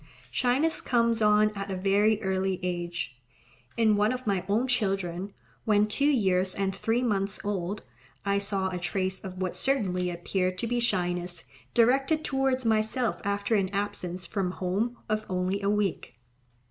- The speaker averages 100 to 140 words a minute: No, average, 160 wpm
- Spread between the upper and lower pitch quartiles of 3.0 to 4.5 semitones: Yes, average, 3.4 semitones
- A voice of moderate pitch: No, high, 200 Hz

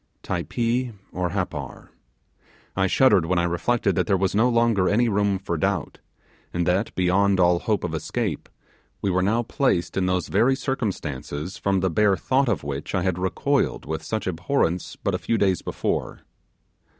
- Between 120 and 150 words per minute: No, average, 175 wpm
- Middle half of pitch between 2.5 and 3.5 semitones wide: No, average, 3.9 semitones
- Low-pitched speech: Yes, very low, 95 Hz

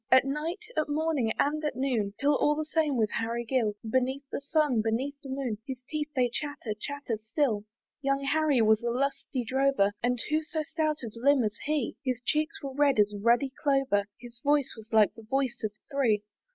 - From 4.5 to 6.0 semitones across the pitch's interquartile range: No, average, 4.1 semitones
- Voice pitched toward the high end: Yes, very high, 265 Hz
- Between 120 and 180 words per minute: No, average, 200 wpm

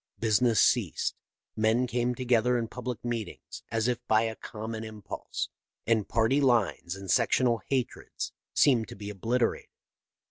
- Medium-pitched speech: No, low, 115 Hz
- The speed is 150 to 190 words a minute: No, average, 140 wpm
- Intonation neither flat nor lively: No, narrow, 2.1 semitones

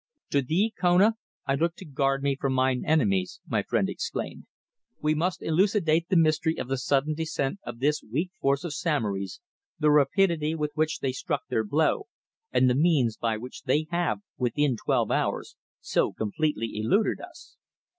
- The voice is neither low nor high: Yes, medium, 150 Hz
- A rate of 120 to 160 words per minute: No, average, 170 wpm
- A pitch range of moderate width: Yes, average, 3.9 semitones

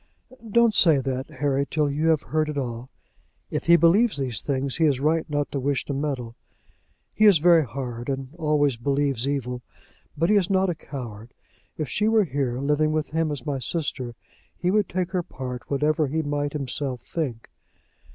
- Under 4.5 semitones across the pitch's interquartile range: Yes, average, 3.6 semitones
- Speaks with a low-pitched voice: No, medium, 145 Hz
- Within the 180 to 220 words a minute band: Yes, average, 190 wpm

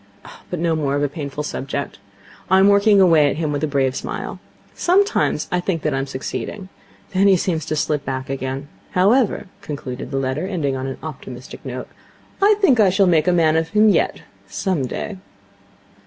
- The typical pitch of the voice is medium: Yes, medium, 155 Hz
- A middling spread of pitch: No, wide, 5.7 semitones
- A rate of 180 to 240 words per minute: Yes, average, 200 wpm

